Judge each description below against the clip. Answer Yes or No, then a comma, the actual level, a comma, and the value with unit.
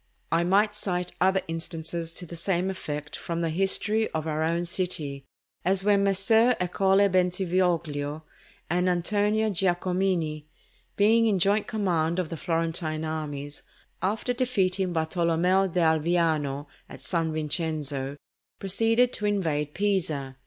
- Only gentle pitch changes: No, average, 3.5 semitones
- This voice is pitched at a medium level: Yes, medium, 175 Hz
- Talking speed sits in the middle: No, slow, 125 wpm